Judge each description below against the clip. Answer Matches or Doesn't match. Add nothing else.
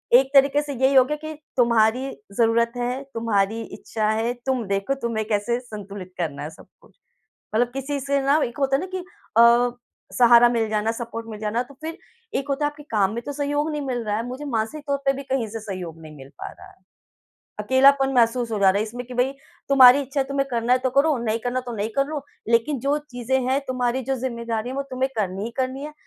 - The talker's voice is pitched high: Matches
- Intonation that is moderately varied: Matches